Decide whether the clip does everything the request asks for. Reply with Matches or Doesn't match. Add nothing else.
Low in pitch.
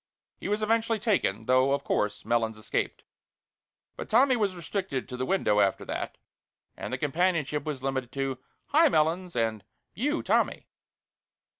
Doesn't match